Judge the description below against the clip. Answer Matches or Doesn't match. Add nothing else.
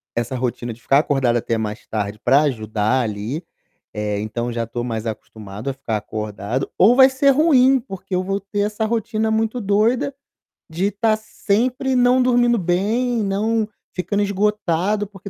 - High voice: Matches